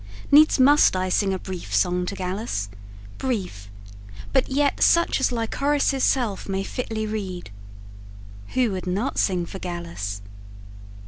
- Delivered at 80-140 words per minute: Yes, slow, 135 wpm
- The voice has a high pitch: Yes, high, 195 Hz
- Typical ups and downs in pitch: No, wide, 6.2 semitones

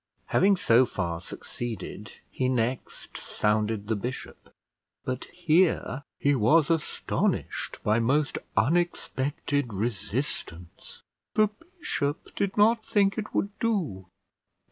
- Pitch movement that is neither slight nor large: No, wide, 7.9 semitones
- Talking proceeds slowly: Yes, slow, 105 wpm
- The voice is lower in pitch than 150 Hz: Yes, low, 135 Hz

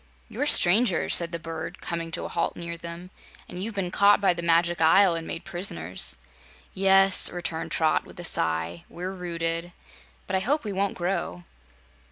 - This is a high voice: No, medium, 175 Hz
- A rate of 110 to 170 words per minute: No, average, 180 wpm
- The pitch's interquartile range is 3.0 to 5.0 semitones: No, narrow, 2.5 semitones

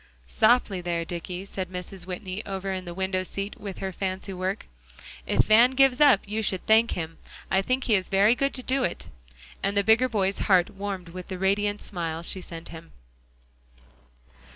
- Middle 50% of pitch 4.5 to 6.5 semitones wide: No, average, 2.8 semitones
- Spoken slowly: No, average, 185 wpm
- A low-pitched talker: No, high, 195 Hz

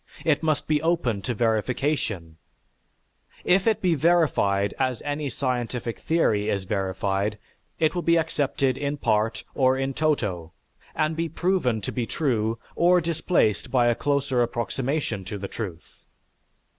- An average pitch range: No, wide, 6.4 semitones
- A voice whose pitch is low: Yes, low, 130 Hz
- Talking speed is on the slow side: No, average, 145 wpm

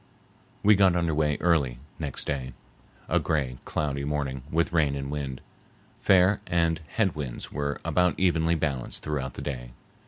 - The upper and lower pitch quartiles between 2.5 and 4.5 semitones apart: Yes, average, 3.6 semitones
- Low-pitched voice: Yes, very low, 75 Hz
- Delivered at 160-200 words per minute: No, average, 150 wpm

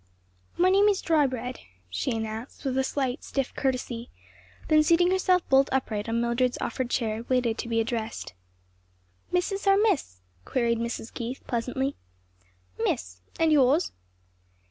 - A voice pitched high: Yes, very high, 255 Hz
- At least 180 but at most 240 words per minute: No, average, 140 wpm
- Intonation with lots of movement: No, average, 4.9 semitones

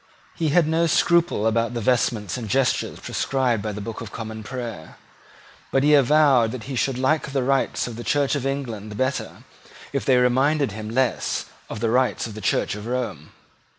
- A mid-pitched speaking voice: No, low, 125 Hz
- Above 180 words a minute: Yes, average, 190 wpm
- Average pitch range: Yes, average, 3.6 semitones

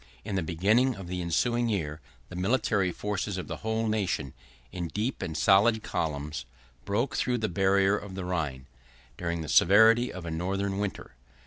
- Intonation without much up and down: No, average, 4.3 semitones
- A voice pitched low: Yes, very low, 95 Hz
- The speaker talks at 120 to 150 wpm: No, average, 175 wpm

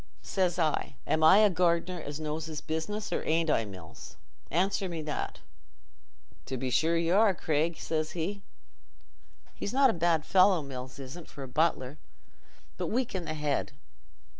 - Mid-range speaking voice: Yes, medium, 160 Hz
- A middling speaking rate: Yes, average, 165 wpm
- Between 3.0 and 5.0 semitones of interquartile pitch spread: Yes, average, 3.4 semitones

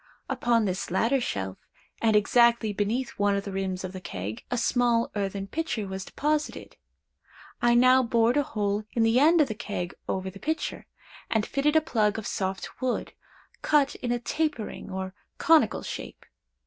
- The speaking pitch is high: Yes, high, 225 Hz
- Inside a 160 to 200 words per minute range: Yes, average, 175 wpm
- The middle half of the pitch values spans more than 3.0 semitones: Yes, average, 4.5 semitones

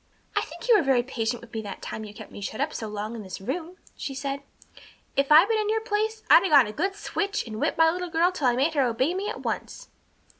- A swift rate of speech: Yes, fast, 270 wpm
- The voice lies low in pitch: No, very high, 285 Hz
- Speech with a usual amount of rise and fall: No, wide, 8.3 semitones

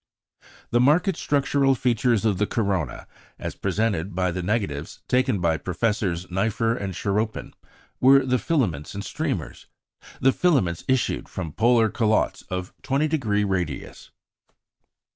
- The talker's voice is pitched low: Yes, low, 110 Hz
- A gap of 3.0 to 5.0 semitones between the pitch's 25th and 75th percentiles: No, wide, 5.5 semitones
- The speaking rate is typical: No, slow, 130 wpm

